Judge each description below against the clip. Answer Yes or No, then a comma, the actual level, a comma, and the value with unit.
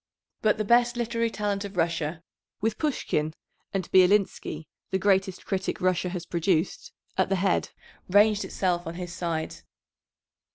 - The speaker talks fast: No, average, 140 wpm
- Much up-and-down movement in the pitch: No, average, 3.3 semitones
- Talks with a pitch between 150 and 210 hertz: Yes, high, 190 Hz